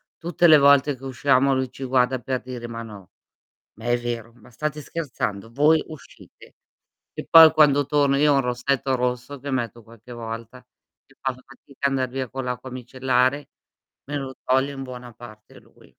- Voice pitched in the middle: No, low, 130 Hz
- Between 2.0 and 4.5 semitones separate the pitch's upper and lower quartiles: Yes, narrow, 2.4 semitones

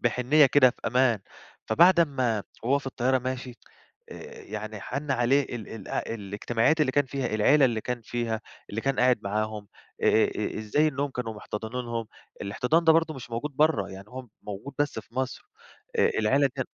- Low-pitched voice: Yes, low, 125 Hz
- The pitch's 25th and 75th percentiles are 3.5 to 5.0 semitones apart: Yes, average, 4.0 semitones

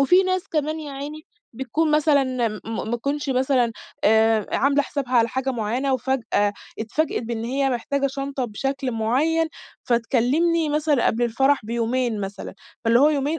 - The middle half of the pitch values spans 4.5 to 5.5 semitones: No, average, 3.9 semitones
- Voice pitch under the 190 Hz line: No, very high, 265 Hz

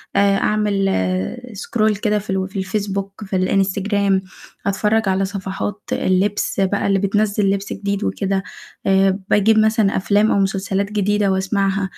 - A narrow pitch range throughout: Yes, narrow, 1.3 semitones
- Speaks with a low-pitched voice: No, high, 200 Hz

